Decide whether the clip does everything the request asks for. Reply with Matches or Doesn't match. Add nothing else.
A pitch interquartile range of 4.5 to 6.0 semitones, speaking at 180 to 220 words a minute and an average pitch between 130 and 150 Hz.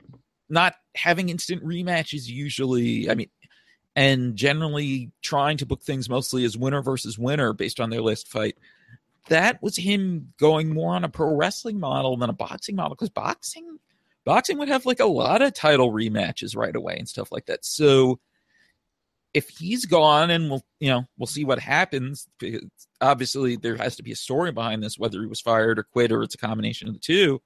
Matches